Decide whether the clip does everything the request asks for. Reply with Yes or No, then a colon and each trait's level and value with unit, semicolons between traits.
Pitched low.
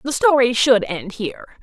No: high, 240 Hz